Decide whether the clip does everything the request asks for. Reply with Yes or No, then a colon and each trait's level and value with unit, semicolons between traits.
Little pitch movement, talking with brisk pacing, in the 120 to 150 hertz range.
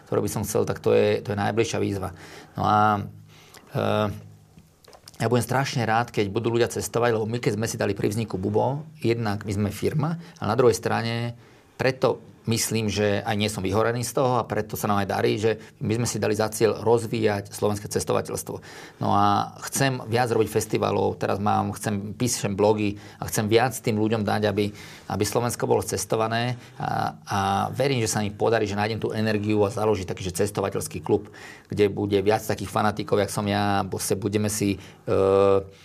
No: narrow, 2.1 semitones; fast, 195 wpm; low, 105 Hz